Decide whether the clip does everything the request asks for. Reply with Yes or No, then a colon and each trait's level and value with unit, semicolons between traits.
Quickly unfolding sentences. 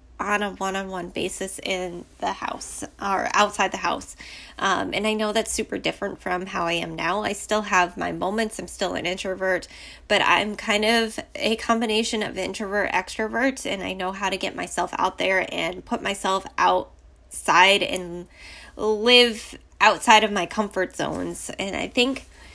No: average, 175 wpm